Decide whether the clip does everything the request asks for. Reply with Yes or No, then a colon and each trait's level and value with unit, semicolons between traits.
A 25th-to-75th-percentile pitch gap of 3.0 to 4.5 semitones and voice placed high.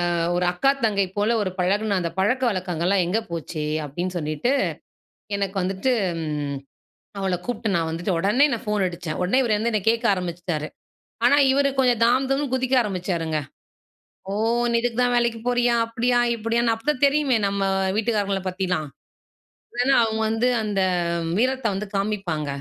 No: average, 4.9 semitones; high, 205 Hz